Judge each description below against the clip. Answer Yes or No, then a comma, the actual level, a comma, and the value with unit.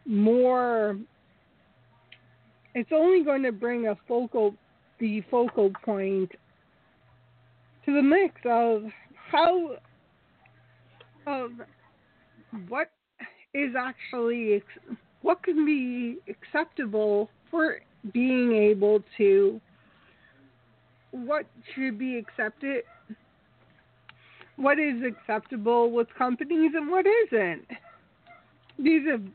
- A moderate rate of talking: No, slow, 85 wpm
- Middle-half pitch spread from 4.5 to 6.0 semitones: Yes, wide, 5.4 semitones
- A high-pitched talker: Yes, high, 240 Hz